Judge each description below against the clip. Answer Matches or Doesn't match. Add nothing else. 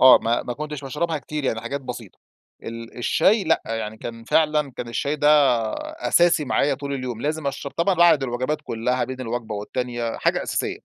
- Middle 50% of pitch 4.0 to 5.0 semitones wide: Matches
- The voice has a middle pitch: Doesn't match